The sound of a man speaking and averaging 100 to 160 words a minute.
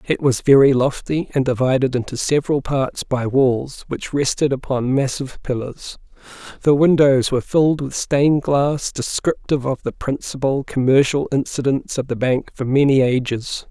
Yes: male; average, 155 wpm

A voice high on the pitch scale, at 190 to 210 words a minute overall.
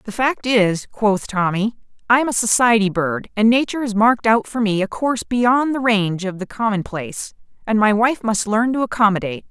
Yes: high, 220 Hz; average, 200 wpm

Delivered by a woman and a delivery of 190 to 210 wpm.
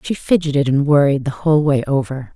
Yes: female; fast, 205 wpm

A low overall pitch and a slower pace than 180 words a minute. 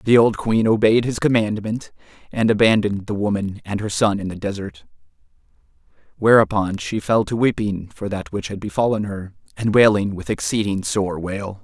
Yes: low, 105 Hz; average, 170 wpm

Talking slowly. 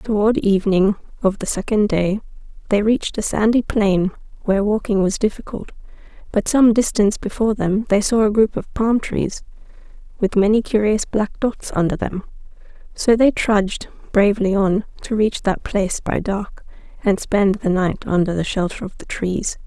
No: average, 170 wpm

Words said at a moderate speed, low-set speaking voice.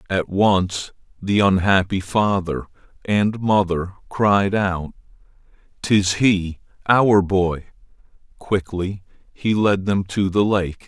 No: slow, 110 wpm; low, 100 Hz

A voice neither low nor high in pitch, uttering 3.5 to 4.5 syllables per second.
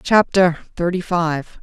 Yes: medium, 175 Hz; 3.7 syllables/s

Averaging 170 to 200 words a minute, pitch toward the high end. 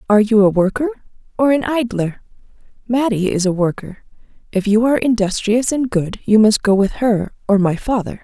Yes: average, 180 wpm; high, 220 Hz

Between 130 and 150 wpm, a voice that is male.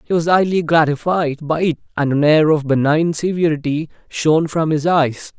No: average, 180 wpm; male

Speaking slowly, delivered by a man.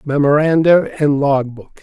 Yes: slow, 130 wpm; male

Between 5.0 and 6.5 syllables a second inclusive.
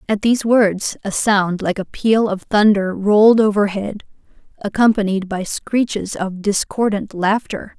No: 4.3 syllables/s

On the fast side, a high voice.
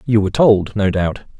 No: fast, 215 wpm; low, 105 Hz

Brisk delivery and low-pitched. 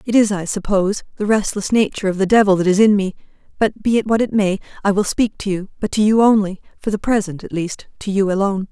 No: fast, 255 wpm; high, 200 Hz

